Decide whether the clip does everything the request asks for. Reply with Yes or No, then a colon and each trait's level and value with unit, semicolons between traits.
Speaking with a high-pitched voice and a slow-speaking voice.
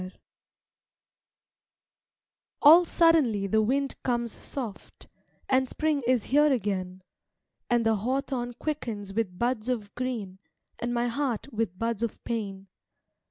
Yes: high, 235 Hz; slow, 120 wpm